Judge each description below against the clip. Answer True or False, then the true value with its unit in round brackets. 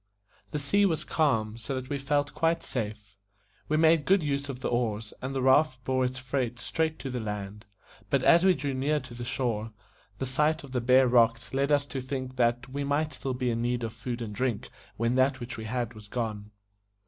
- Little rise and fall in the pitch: False (3.1 semitones)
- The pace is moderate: False (220 wpm)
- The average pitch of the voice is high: False (130 Hz)